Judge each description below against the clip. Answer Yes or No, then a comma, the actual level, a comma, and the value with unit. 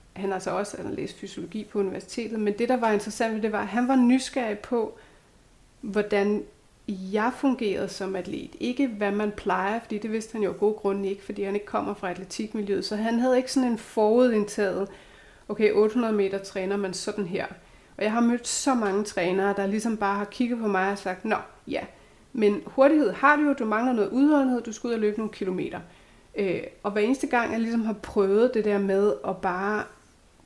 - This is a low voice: No, high, 210 Hz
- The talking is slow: No, average, 210 wpm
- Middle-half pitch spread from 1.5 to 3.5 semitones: Yes, average, 2.8 semitones